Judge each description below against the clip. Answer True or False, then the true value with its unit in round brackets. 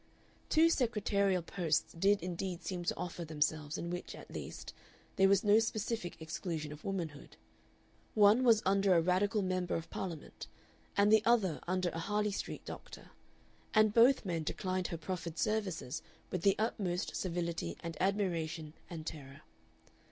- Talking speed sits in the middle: True (150 wpm)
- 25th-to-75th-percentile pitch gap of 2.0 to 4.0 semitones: True (3.7 semitones)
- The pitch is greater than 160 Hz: True (185 Hz)